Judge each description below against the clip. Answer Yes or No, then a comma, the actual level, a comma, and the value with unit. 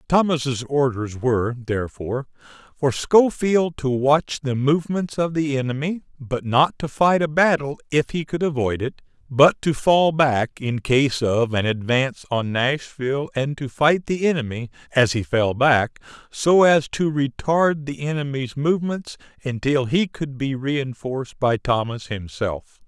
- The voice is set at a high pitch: No, medium, 140 Hz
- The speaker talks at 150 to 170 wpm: Yes, average, 155 wpm